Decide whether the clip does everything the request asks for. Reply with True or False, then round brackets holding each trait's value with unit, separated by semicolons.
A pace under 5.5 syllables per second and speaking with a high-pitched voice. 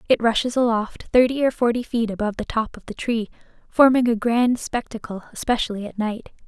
False (5.6 syllables/s; 230 Hz)